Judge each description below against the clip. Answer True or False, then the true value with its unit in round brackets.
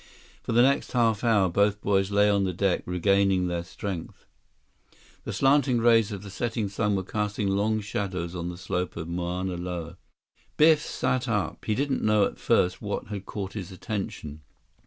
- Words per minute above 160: True (180 wpm)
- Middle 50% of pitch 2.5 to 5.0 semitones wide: True (3.1 semitones)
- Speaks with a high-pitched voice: False (100 Hz)